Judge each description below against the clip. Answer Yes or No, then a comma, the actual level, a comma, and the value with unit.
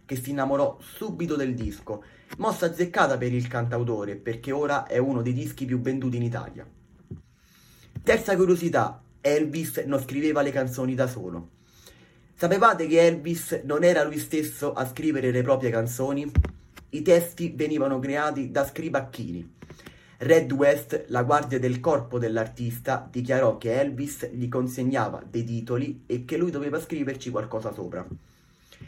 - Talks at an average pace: Yes, average, 145 wpm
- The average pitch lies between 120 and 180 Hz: Yes, low, 135 Hz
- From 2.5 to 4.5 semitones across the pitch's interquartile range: Yes, average, 3.8 semitones